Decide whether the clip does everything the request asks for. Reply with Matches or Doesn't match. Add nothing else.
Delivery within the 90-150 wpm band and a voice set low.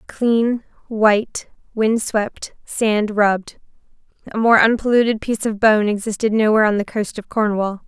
Doesn't match